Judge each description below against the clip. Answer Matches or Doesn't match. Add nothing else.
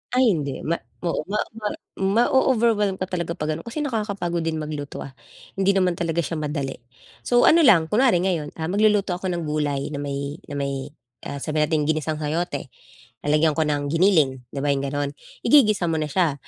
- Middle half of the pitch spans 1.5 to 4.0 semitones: Doesn't match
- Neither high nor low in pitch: Matches